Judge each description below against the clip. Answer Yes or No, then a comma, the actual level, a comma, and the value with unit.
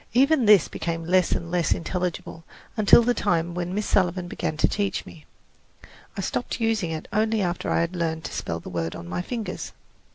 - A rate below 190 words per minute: No, average, 195 wpm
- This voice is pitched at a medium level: Yes, medium, 180 Hz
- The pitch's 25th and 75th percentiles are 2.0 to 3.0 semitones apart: No, average, 4.2 semitones